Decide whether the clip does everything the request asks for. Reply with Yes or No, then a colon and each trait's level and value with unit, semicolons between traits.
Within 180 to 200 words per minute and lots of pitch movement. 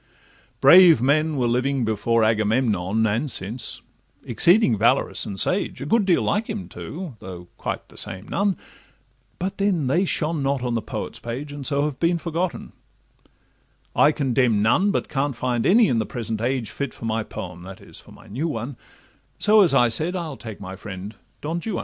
Yes: average, 185 wpm; wide, 7.0 semitones